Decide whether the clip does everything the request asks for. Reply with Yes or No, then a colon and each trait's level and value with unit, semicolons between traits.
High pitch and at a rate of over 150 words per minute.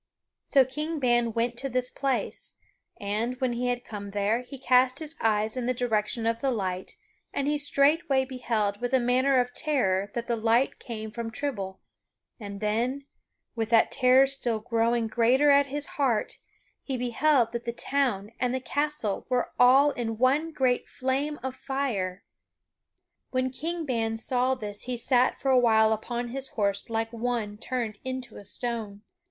Yes: high, 245 Hz; average, 170 wpm